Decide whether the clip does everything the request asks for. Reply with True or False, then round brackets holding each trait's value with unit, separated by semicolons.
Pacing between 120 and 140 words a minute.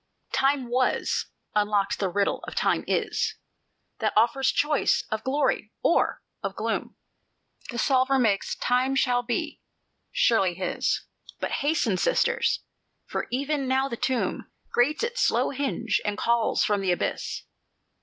True (135 wpm)